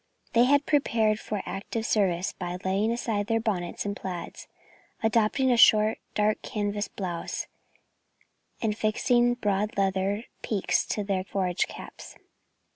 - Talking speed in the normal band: No, slow, 130 wpm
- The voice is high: Yes, high, 210 Hz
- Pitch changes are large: No, narrow, 2.6 semitones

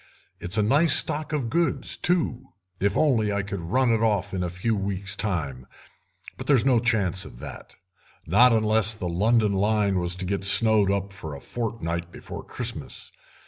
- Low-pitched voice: Yes, low, 105 Hz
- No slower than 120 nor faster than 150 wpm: No, average, 175 wpm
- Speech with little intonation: No, average, 3.8 semitones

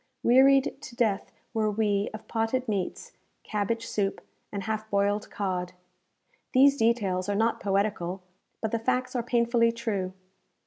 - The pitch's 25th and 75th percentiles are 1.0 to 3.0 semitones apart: Yes, average, 2.7 semitones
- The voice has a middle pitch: No, high, 220 Hz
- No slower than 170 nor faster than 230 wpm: No, average, 140 wpm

